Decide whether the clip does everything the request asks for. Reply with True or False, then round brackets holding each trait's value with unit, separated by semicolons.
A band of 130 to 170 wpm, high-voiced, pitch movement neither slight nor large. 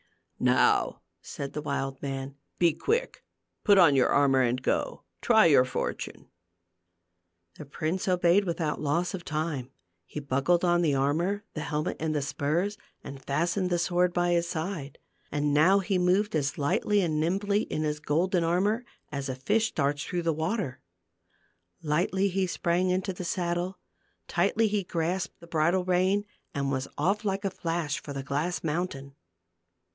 False (165 wpm; 170 Hz; 4.1 semitones)